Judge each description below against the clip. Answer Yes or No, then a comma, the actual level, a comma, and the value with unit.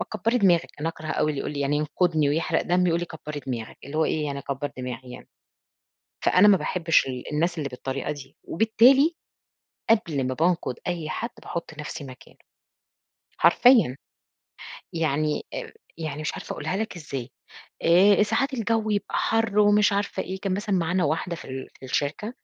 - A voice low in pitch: No, medium, 165 Hz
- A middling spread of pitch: No, wide, 5.9 semitones